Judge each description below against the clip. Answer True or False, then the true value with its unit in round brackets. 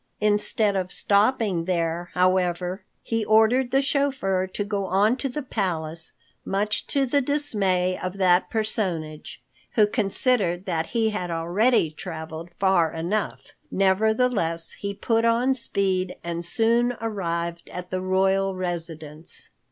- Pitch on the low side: False (195 Hz)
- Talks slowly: True (130 wpm)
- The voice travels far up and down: False (4.2 semitones)